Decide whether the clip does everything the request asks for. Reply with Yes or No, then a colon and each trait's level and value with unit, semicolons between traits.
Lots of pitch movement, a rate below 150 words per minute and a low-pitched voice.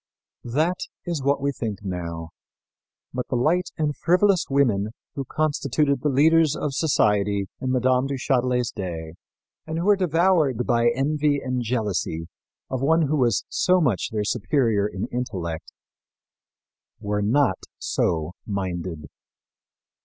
Yes: wide, 6.5 semitones; slow, 135 wpm; low, 125 Hz